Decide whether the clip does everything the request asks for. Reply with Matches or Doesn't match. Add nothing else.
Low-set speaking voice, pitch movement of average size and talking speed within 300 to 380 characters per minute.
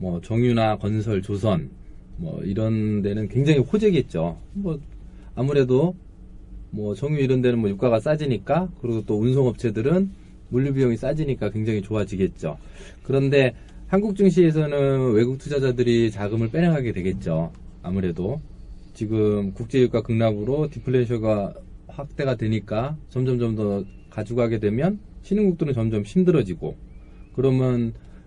Matches